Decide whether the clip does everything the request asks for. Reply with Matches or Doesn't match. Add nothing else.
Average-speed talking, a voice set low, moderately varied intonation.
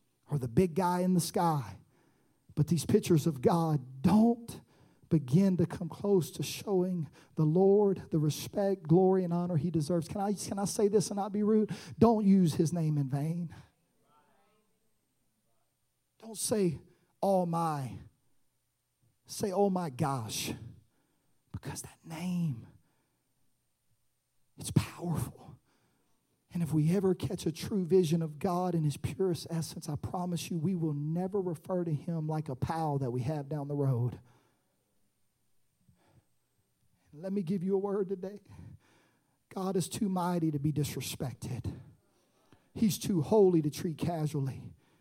Doesn't match